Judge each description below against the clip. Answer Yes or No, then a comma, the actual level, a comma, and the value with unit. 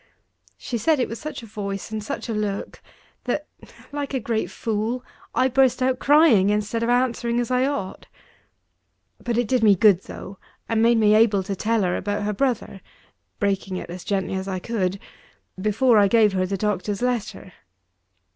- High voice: Yes, high, 220 Hz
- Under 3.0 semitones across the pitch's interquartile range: No, average, 3.6 semitones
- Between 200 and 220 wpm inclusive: No, average, 185 wpm